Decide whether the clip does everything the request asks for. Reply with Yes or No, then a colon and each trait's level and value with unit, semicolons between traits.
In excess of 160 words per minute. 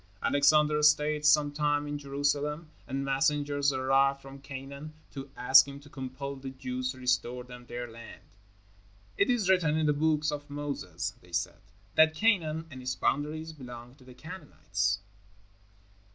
No: average, 155 wpm